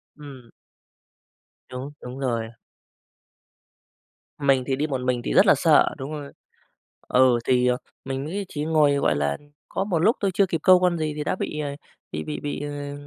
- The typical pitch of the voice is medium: Yes, medium, 145 Hz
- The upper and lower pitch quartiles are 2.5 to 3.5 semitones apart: Yes, average, 3.2 semitones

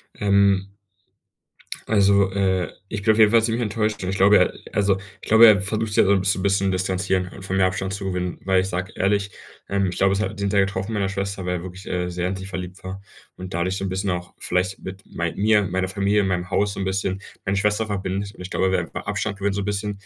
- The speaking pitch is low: Yes, very low, 95 Hz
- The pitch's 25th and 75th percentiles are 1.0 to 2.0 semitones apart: Yes, narrow, 1.3 semitones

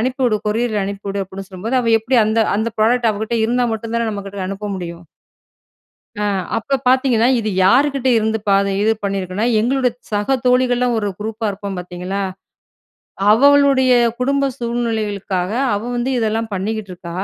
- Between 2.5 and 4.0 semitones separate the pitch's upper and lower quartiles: Yes, average, 3.6 semitones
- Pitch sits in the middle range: No, high, 220 Hz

